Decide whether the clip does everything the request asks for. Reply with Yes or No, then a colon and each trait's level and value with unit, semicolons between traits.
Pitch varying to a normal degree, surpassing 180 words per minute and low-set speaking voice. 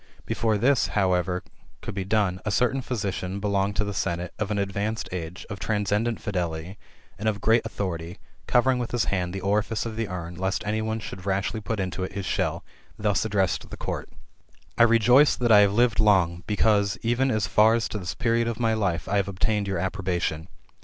Yes: average, 3.0 semitones; fast, 205 wpm; low, 100 Hz